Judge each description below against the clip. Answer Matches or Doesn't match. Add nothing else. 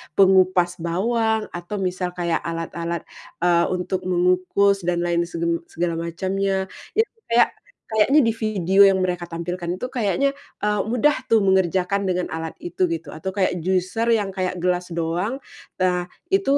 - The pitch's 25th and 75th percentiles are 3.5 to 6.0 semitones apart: Doesn't match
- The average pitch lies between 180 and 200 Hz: Matches